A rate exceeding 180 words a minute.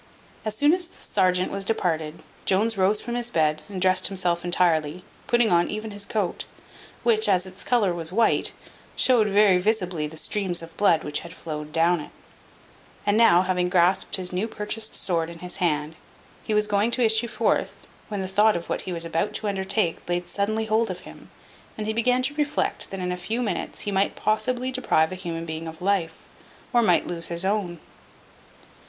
Yes: average, 195 wpm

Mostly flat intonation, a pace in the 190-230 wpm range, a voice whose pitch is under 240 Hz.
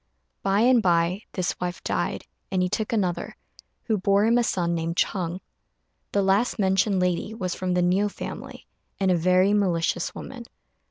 No: narrow, 2.3 semitones; average, 170 wpm; high, 190 Hz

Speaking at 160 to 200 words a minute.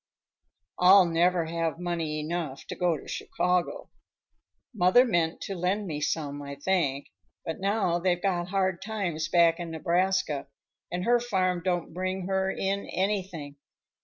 No: average, 145 wpm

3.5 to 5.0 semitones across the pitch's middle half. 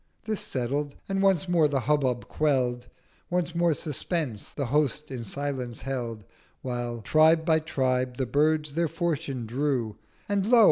Yes: average, 4.2 semitones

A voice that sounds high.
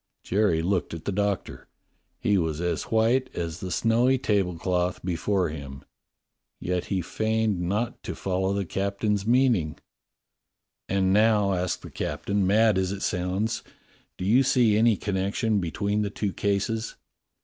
No: low, 100 Hz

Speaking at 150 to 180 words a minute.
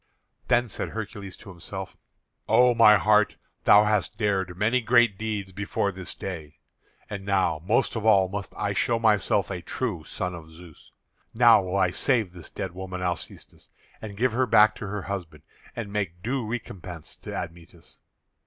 Yes: average, 170 wpm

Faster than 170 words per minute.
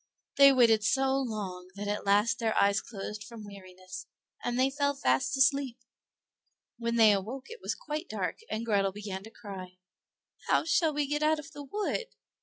Yes: average, 180 wpm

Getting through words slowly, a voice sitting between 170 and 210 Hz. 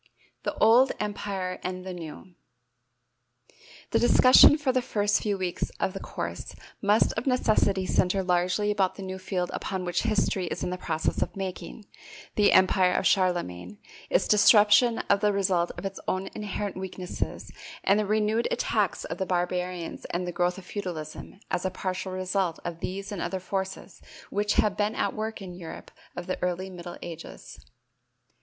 No: average, 175 wpm; high, 190 Hz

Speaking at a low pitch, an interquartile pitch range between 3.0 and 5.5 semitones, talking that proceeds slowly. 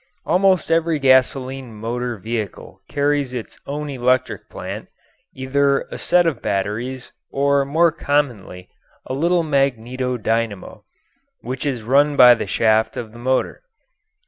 Yes: low, 130 Hz; average, 3.4 semitones; slow, 130 wpm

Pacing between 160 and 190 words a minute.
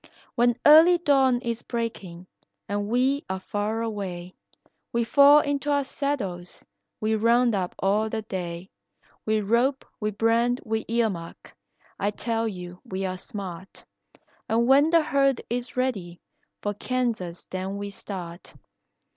No: average, 140 wpm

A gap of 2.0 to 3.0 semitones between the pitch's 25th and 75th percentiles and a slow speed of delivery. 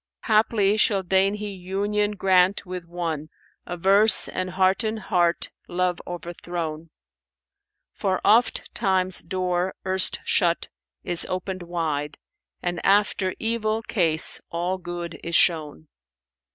Yes: narrow, 2.5 semitones; slow, 115 wpm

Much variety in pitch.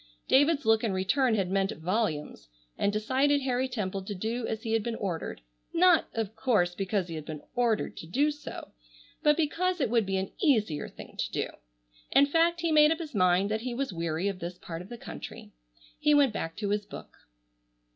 Yes: wide, 6.6 semitones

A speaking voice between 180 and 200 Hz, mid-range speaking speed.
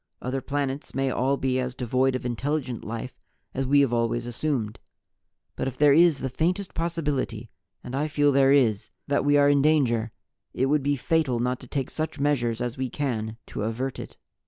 No: low, 135 Hz; average, 195 wpm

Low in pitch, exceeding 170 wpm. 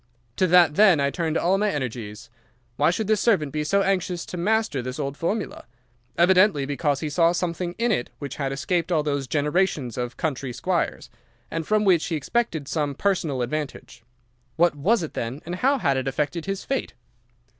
No: medium, 160 Hz; average, 190 wpm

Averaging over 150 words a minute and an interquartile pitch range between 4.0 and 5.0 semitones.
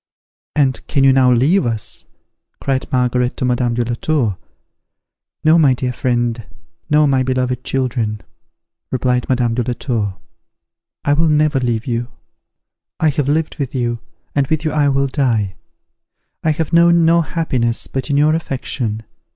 No: average, 160 wpm; average, 3.6 semitones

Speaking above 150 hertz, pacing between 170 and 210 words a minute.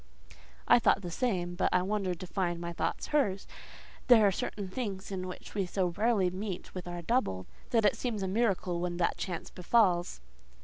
Yes: high, 190 Hz; average, 190 wpm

